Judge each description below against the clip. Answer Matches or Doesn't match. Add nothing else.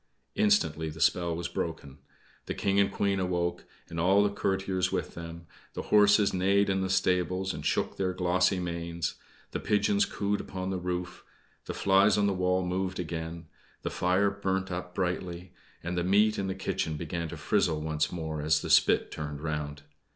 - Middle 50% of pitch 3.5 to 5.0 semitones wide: Doesn't match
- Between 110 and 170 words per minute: Doesn't match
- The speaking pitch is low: Matches